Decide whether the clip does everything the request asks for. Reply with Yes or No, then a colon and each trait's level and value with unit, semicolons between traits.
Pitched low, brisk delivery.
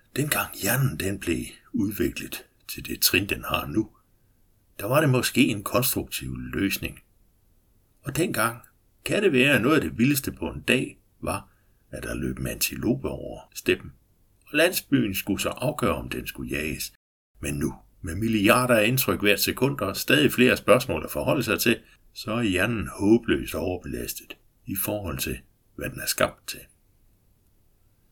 No: low, 100 Hz; average, 165 wpm